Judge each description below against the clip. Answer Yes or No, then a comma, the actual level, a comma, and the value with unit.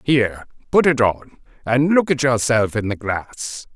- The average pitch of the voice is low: Yes, low, 120 Hz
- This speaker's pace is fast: No, average, 175 wpm